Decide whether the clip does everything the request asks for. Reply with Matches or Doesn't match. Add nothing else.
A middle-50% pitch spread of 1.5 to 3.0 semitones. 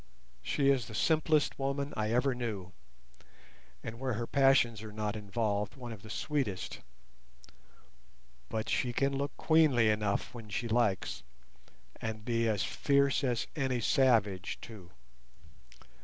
Doesn't match